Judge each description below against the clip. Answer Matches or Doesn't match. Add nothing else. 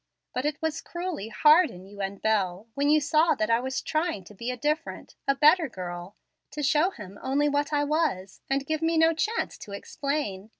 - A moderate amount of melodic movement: Doesn't match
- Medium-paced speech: Doesn't match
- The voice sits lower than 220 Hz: Doesn't match